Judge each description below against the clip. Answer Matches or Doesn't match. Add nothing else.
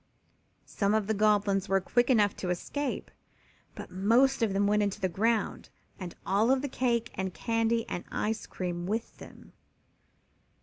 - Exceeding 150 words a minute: Matches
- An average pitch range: Matches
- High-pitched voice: Matches